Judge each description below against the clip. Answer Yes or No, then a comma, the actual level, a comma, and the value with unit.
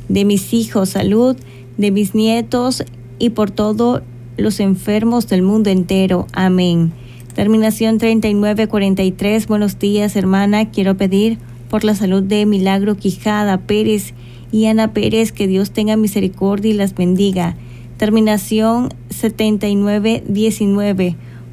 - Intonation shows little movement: Yes, narrow, 2.3 semitones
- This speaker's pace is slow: Yes, slow, 115 wpm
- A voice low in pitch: No, high, 205 Hz